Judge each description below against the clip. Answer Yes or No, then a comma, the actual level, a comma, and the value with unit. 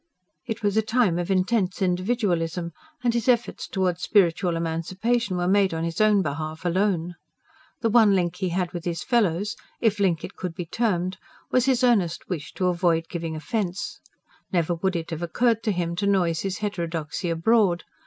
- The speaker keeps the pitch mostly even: No, average, 3.8 semitones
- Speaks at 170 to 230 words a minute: Yes, average, 180 wpm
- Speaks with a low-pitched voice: No, medium, 185 Hz